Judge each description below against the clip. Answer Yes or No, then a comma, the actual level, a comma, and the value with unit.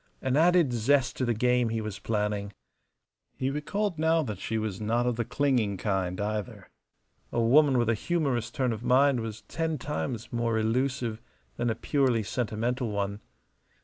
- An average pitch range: Yes, average, 3.8 semitones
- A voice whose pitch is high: No, low, 120 Hz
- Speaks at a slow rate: No, average, 170 wpm